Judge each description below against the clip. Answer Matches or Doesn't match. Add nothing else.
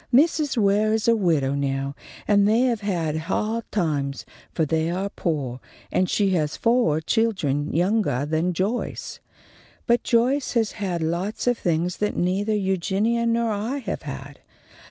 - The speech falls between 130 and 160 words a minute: Matches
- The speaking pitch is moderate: Doesn't match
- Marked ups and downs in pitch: Matches